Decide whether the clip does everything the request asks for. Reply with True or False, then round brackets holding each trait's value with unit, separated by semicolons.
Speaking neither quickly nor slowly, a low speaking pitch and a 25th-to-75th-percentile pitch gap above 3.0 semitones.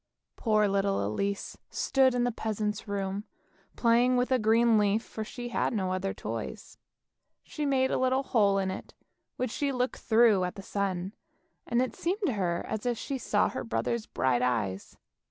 False (180 wpm; 215 Hz; 4.1 semitones)